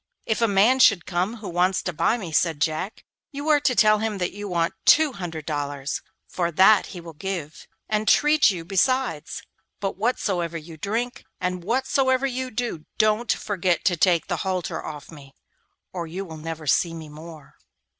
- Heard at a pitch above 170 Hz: Yes, medium, 185 Hz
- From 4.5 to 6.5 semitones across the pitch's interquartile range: Yes, average, 5.2 semitones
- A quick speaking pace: No, average, 185 wpm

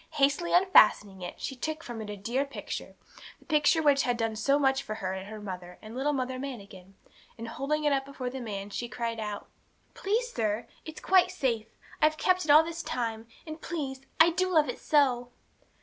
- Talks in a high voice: Yes, very high, 265 Hz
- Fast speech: Yes, fast, 210 wpm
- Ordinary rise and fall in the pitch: No, wide, 5.7 semitones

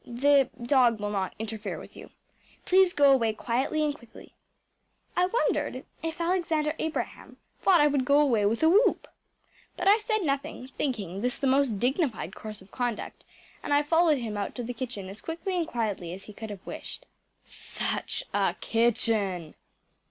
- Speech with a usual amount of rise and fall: No, wide, 6.2 semitones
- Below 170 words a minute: No, average, 175 wpm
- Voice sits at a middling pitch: No, very high, 260 Hz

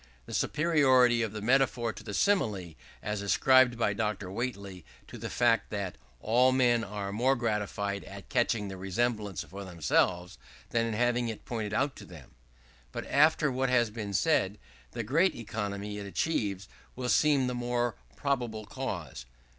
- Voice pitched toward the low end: Yes, low, 115 Hz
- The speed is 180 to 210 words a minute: No, average, 160 wpm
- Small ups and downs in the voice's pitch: No, average, 3.9 semitones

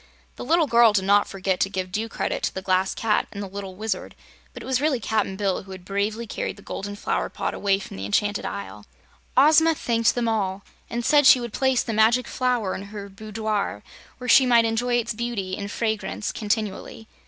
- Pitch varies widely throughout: No, average, 3.4 semitones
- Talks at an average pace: No, fast, 210 wpm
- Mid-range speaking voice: No, high, 215 Hz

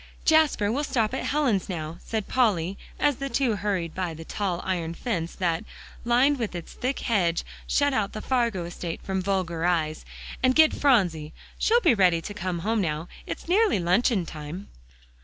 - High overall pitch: Yes, high, 195 Hz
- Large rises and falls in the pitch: Yes, wide, 6.6 semitones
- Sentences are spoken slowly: No, average, 175 wpm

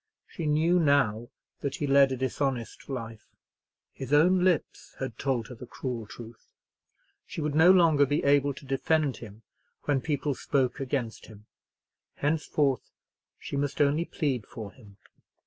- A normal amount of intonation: Yes, average, 3.4 semitones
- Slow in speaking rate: No, average, 150 wpm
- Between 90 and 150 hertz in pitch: Yes, medium, 140 Hz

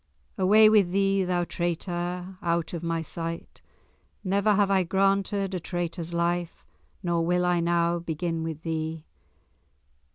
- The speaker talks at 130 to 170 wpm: Yes, slow, 135 wpm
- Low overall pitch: No, medium, 175 Hz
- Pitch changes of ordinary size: No, narrow, 2.2 semitones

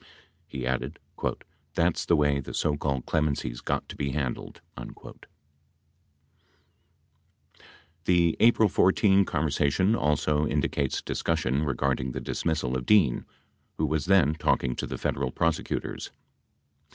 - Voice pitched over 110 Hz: No, very low, 75 Hz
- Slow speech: Yes, slow, 120 wpm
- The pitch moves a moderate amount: Yes, average, 3.6 semitones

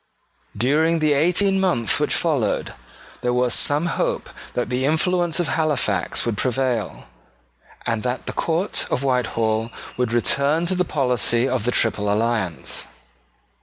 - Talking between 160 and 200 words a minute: No, average, 140 wpm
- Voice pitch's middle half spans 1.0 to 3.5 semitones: No, wide, 5.4 semitones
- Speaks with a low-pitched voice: Yes, low, 130 Hz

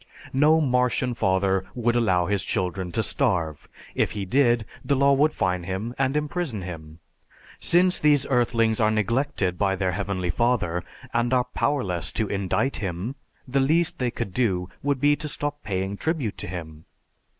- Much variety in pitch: Yes, wide, 6.5 semitones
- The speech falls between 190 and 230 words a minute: No, average, 165 wpm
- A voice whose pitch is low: Yes, low, 110 Hz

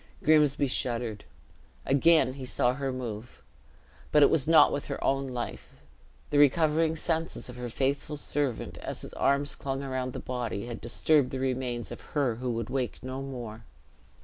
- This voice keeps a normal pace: Yes, average, 170 wpm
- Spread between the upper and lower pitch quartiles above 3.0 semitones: No, average, 2.7 semitones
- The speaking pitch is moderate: No, low, 130 Hz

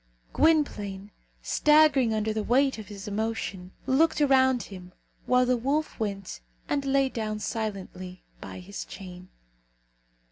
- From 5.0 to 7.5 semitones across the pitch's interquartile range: Yes, average, 5.3 semitones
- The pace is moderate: No, slow, 130 wpm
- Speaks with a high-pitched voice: Yes, high, 220 Hz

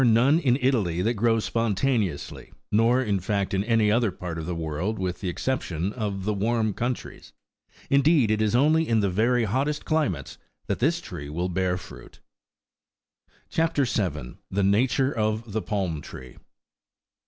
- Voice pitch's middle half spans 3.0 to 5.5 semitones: Yes, average, 4.8 semitones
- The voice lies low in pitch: Yes, low, 105 Hz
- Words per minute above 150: Yes, average, 165 wpm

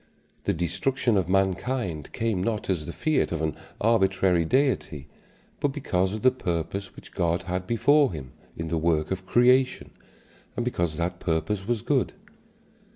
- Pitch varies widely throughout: Yes, wide, 5.9 semitones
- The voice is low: Yes, very low, 95 Hz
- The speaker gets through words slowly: No, average, 155 wpm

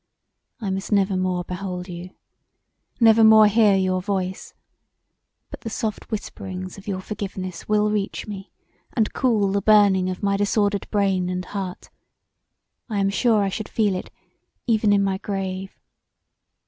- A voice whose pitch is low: No, high, 200 Hz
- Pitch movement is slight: Yes, narrow, 2.2 semitones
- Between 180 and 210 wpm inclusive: No, average, 150 wpm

